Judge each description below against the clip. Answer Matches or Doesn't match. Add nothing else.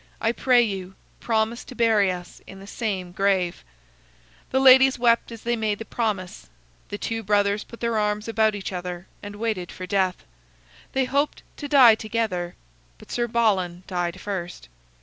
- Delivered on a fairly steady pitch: Doesn't match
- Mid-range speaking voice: Doesn't match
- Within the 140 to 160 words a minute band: Doesn't match